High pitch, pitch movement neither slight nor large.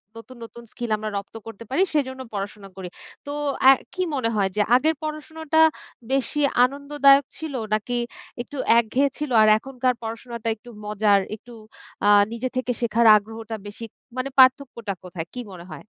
Yes: high, 240 Hz; average, 4.2 semitones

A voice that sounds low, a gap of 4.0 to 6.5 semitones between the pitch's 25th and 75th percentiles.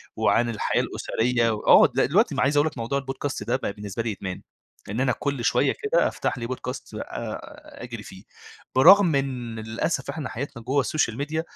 No: low, 125 Hz; average, 3.5 semitones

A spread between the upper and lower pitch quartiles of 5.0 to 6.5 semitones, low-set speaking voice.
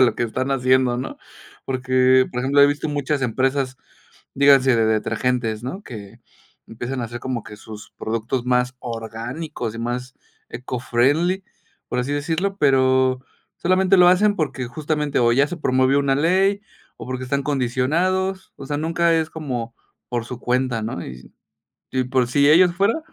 No: average, 3.5 semitones; low, 130 Hz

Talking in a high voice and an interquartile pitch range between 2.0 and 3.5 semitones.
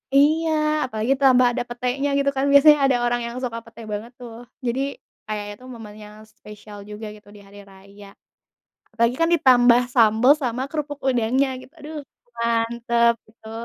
Yes: high, 235 Hz; average, 3.1 semitones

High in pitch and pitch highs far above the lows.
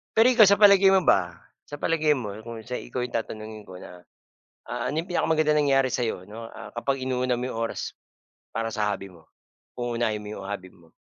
No: low, 120 Hz; wide, 5.7 semitones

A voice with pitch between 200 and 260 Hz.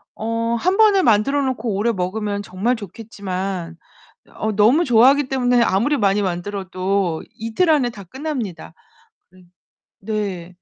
Yes: high, 215 Hz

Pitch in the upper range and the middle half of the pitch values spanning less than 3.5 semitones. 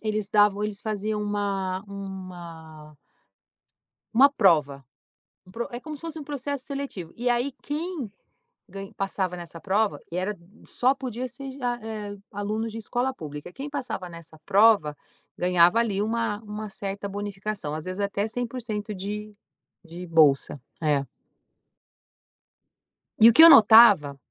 No: high, 205 Hz; average, 4.3 semitones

